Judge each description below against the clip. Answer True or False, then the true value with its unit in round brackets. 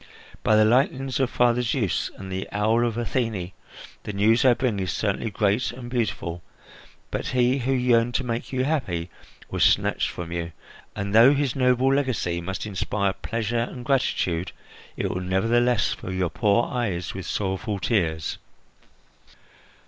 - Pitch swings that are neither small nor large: True (4.6 semitones)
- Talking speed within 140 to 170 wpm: True (155 wpm)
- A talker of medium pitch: False (115 Hz)